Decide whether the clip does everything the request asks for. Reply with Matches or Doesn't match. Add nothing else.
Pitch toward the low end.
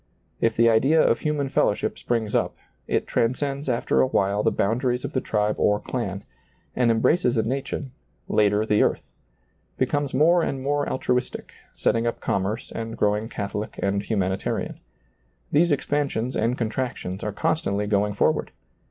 Matches